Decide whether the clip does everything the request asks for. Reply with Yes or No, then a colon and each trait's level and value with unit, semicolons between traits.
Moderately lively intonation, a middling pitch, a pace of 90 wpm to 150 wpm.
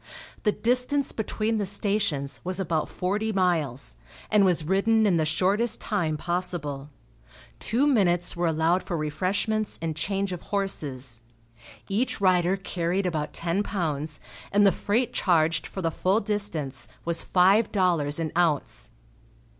Yes: average, 4.2 semitones; medium, 180 Hz; average, 140 wpm